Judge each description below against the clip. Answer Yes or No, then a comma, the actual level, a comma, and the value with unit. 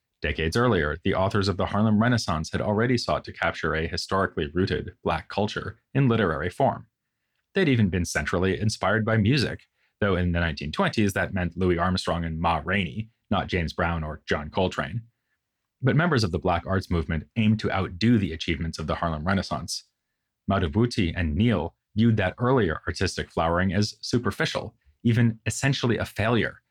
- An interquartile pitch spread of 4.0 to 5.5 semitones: Yes, average, 4.6 semitones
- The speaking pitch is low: Yes, very low, 95 Hz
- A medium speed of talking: Yes, average, 170 wpm